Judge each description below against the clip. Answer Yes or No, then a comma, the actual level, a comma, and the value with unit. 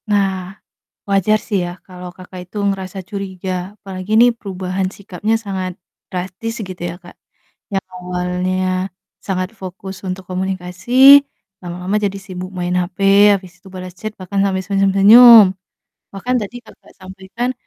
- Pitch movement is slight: Yes, narrow, 1.7 semitones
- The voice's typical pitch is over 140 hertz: Yes, high, 190 Hz